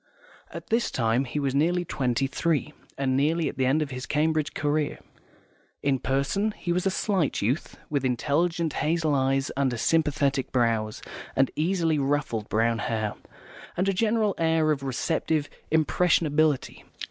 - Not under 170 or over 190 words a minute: No, average, 150 wpm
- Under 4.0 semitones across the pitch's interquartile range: Yes, average, 3.5 semitones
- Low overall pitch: No, medium, 145 Hz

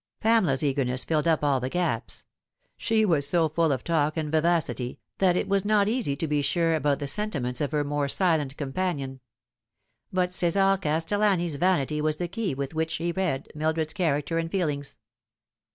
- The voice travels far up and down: No, average, 4.0 semitones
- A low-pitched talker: No, medium, 160 Hz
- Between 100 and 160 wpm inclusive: No, average, 175 wpm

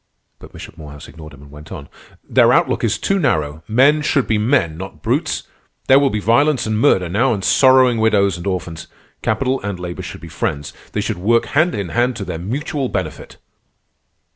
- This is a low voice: Yes, low, 105 Hz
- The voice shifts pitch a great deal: Yes, wide, 7.3 semitones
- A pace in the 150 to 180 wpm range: No, average, 200 wpm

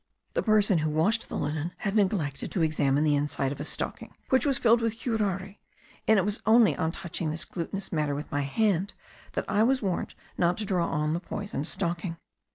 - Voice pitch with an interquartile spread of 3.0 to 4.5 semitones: No, average, 5.3 semitones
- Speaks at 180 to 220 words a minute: Yes, fast, 205 wpm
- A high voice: No, medium, 180 Hz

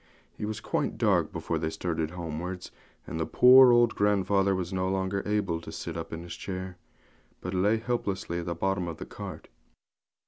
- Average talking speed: Yes, average, 185 wpm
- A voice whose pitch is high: No, very low, 95 Hz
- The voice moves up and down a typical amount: Yes, average, 3.1 semitones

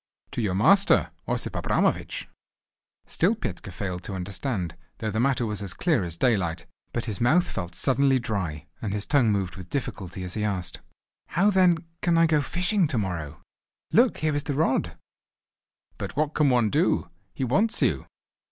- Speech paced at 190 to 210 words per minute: No, average, 175 wpm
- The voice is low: Yes, low, 115 Hz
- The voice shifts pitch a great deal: Yes, wide, 8.1 semitones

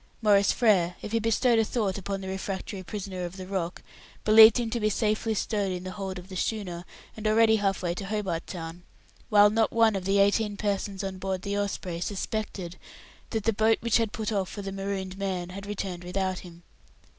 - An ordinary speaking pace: No, fast, 210 wpm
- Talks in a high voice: Yes, high, 200 Hz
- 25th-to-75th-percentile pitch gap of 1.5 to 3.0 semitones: Yes, narrow, 2.4 semitones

